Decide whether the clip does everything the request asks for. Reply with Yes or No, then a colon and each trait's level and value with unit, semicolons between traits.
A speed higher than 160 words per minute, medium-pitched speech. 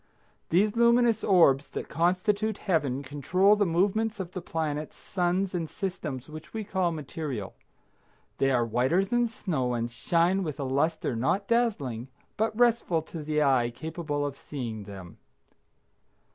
No: average, 145 wpm; medium, 165 Hz